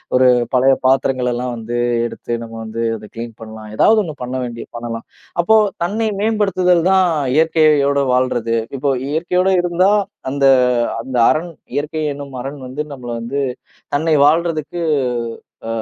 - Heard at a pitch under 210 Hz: Yes, medium, 140 Hz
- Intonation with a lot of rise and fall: Yes, wide, 5.7 semitones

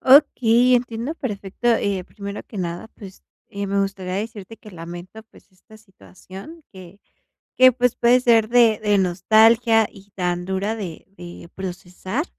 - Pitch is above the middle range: Yes, high, 205 Hz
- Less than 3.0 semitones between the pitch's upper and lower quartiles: No, average, 3.6 semitones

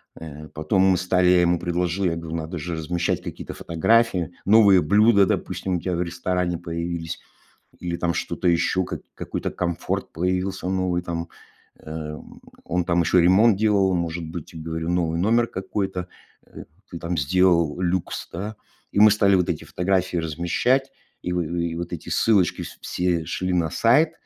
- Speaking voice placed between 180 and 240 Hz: No, very low, 90 Hz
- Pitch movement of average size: No, narrow, 2.1 semitones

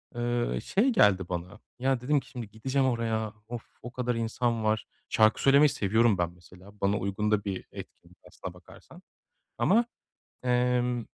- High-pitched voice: No, low, 115 Hz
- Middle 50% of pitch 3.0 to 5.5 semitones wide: Yes, average, 3.3 semitones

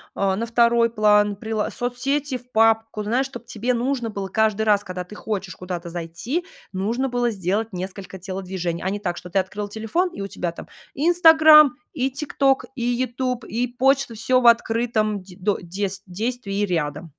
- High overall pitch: Yes, high, 220 Hz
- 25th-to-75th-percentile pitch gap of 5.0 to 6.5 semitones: No, average, 4.3 semitones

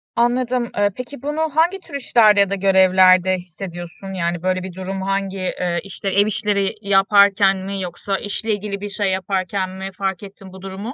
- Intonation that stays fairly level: Yes, narrow, 1.7 semitones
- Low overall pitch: No, high, 195 Hz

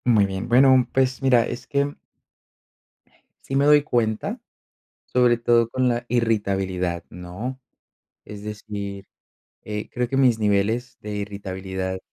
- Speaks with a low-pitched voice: Yes, low, 110 Hz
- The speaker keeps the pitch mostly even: No, average, 3.8 semitones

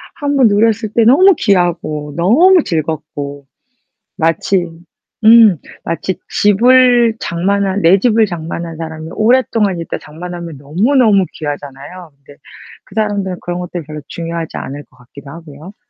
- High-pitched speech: No, medium, 180 Hz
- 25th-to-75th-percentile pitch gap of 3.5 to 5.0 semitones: No, wide, 5.5 semitones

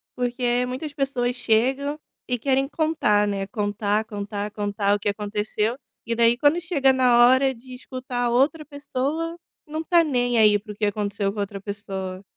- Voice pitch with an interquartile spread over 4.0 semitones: Yes, average, 4.6 semitones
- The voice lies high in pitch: Yes, high, 245 Hz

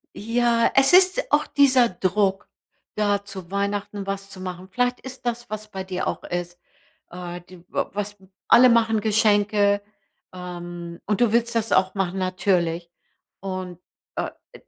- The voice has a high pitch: Yes, high, 200 Hz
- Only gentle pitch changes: No, average, 3.7 semitones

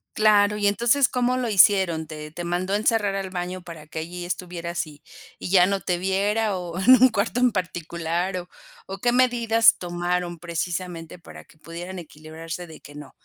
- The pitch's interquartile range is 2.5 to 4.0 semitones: Yes, average, 3.1 semitones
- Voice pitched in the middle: Yes, medium, 180 Hz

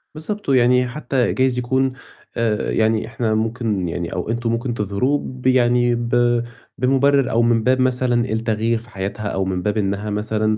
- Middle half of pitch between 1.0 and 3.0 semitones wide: Yes, average, 2.7 semitones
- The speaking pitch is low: Yes, low, 120 Hz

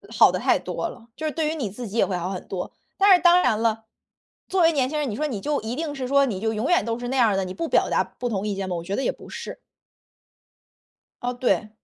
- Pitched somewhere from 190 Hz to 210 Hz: No, high, 245 Hz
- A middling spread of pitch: No, wide, 6.2 semitones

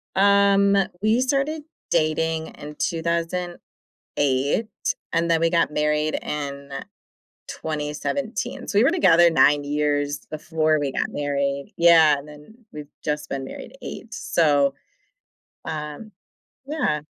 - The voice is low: No, medium, 155 Hz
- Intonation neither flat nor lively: Yes, average, 4.6 semitones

